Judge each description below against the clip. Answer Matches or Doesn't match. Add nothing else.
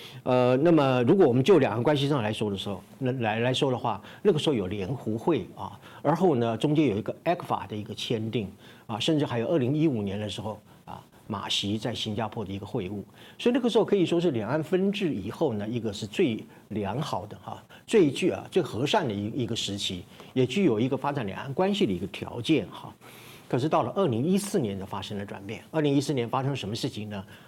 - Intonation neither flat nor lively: Doesn't match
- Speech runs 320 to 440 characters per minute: Matches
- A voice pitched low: Matches